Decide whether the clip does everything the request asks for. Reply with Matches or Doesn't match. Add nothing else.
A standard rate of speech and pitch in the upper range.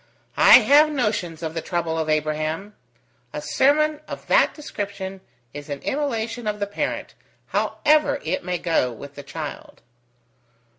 Matches